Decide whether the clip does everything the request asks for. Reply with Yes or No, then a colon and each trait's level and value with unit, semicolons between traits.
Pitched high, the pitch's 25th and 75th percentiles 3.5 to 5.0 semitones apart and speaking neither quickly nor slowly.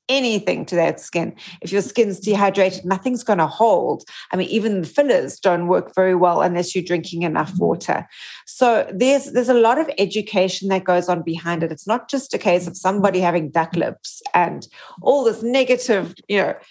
Yes: high, 195 Hz; average, 4.7 semitones; average, 195 wpm